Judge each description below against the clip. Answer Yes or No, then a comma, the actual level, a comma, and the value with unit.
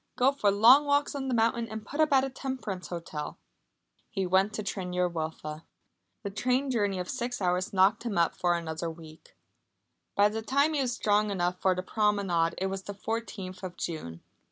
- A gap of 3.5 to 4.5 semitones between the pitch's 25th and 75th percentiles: No, average, 4.9 semitones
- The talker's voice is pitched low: No, high, 200 Hz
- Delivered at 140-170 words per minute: No, average, 200 wpm